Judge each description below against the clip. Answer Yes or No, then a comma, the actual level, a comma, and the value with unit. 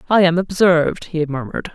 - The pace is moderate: Yes, average, 170 wpm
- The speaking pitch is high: No, medium, 170 Hz